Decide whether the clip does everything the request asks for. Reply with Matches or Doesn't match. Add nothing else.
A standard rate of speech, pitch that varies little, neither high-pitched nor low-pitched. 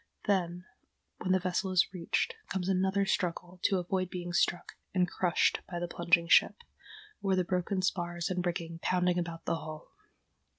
Matches